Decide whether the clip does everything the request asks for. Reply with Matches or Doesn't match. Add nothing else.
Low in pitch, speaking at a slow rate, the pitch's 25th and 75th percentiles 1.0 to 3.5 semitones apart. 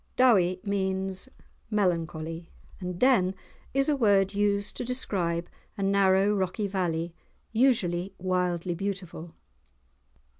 Doesn't match